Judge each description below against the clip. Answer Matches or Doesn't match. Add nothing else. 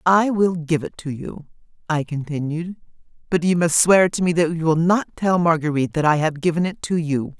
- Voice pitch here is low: Doesn't match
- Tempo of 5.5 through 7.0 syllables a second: Doesn't match